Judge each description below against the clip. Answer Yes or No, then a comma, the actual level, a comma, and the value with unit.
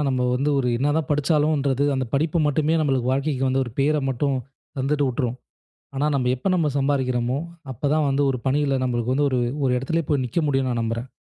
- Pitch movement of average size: No, narrow, 2.3 semitones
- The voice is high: No, low, 135 Hz